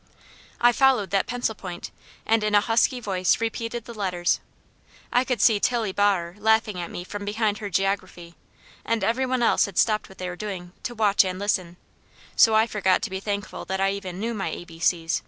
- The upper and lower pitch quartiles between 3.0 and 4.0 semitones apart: Yes, average, 3.3 semitones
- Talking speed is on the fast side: Yes, fast, 210 wpm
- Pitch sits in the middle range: No, high, 205 Hz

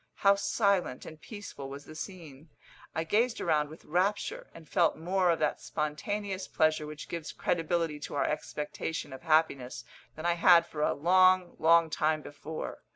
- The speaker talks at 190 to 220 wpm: No, average, 165 wpm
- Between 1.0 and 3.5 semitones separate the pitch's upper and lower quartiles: Yes, average, 3.2 semitones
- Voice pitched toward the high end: No, medium, 165 Hz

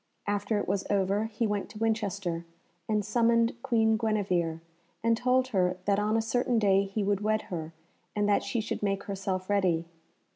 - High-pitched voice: Yes, high, 205 Hz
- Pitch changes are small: Yes, narrow, 2.3 semitones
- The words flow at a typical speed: Yes, average, 180 wpm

